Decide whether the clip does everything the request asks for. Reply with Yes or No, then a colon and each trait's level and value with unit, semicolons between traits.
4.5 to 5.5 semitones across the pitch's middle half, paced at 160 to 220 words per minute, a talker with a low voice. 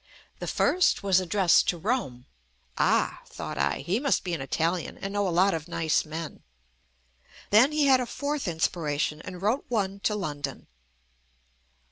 No: average, 5.0 semitones; average, 165 wpm; medium, 185 Hz